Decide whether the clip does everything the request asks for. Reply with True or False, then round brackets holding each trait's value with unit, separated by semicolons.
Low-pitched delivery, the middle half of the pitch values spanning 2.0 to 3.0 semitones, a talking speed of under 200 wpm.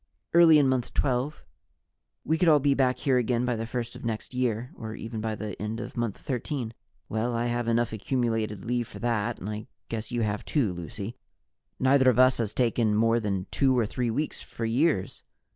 False (120 Hz; 2.7 semitones; 205 wpm)